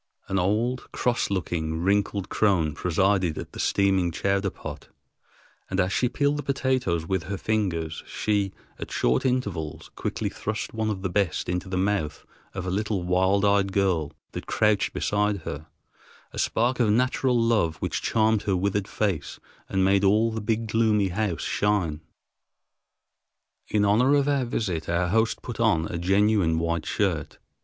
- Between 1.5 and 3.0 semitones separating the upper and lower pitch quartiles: No, average, 3.5 semitones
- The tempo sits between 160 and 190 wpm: Yes, average, 165 wpm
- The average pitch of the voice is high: No, low, 100 Hz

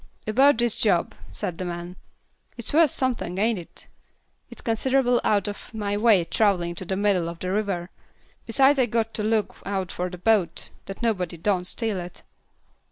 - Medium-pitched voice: No, high, 205 Hz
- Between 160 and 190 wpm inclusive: Yes, average, 175 wpm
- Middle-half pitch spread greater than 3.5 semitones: Yes, average, 4.1 semitones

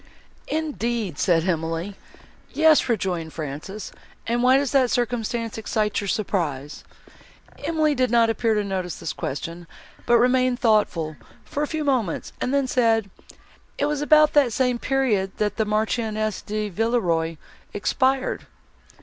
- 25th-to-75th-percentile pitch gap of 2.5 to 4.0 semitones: No, average, 5.1 semitones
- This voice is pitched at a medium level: No, high, 225 Hz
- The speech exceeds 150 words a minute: No, average, 140 wpm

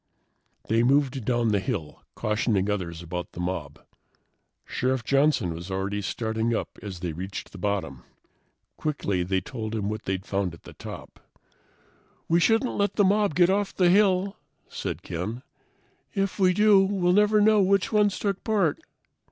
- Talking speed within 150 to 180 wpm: Yes, average, 160 wpm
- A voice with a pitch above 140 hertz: No, low, 120 Hz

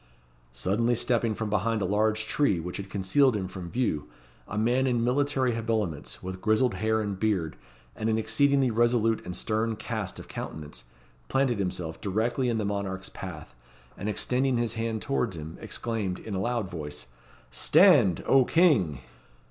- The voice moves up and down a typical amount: Yes, average, 4.0 semitones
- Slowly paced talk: No, average, 165 wpm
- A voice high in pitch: No, low, 110 Hz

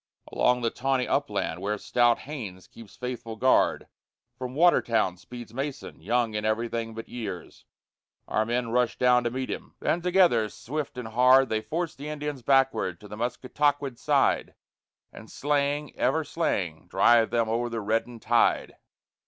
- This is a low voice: Yes, low, 120 Hz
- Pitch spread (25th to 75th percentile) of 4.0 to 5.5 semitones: No, average, 3.2 semitones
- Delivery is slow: No, average, 155 wpm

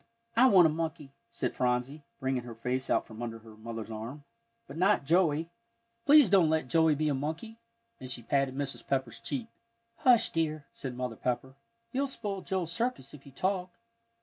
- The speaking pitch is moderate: Yes, medium, 145 Hz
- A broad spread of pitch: Yes, wide, 6.4 semitones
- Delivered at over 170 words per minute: Yes, average, 180 wpm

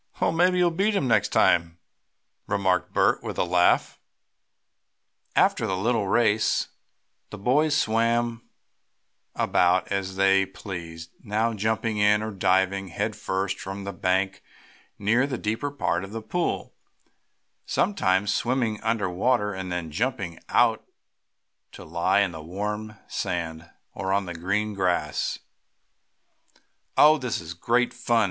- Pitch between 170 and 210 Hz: No, low, 100 Hz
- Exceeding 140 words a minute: No, slow, 135 wpm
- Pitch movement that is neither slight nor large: Yes, average, 3.9 semitones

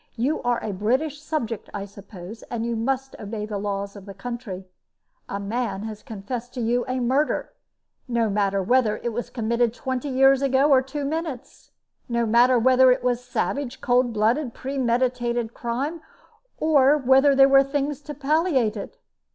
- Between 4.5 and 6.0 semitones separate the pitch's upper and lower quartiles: No, average, 3.4 semitones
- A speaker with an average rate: Yes, average, 170 wpm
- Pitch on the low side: No, high, 245 Hz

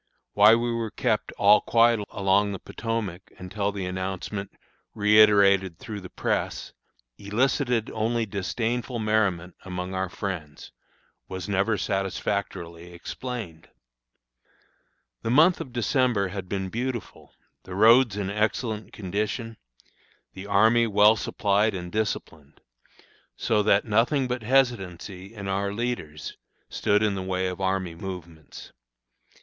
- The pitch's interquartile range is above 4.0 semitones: No, average, 3.2 semitones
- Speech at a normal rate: No, slow, 120 wpm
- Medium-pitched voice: No, low, 100 Hz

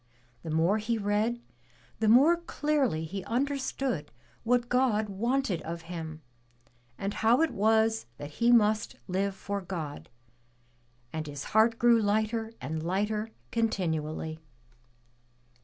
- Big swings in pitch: Yes, wide, 5.7 semitones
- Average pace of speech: No, slow, 125 wpm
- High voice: Yes, high, 210 Hz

